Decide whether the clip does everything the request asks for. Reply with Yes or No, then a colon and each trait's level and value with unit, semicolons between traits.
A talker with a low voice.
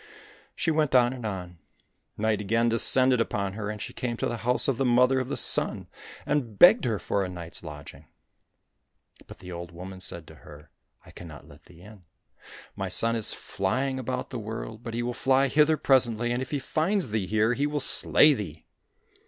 Yes: low, 115 Hz